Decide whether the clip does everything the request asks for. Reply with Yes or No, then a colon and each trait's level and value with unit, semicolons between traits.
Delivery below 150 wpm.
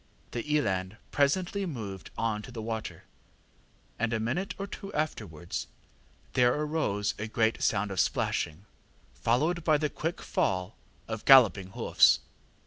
Yes: slow, 135 wpm